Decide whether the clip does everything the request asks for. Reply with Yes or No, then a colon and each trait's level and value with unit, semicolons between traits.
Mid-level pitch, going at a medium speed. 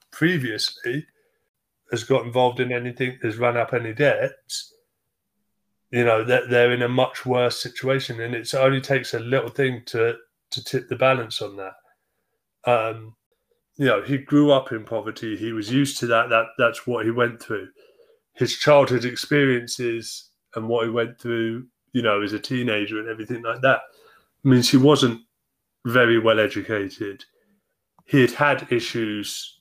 No: low, 120 Hz; average, 165 wpm